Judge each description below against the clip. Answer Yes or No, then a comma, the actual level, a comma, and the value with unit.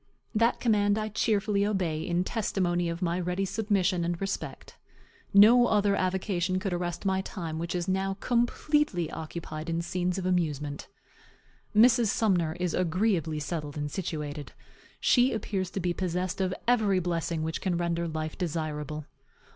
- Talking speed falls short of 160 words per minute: Yes, average, 150 wpm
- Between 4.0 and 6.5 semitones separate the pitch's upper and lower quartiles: No, average, 3.2 semitones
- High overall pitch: No, medium, 180 Hz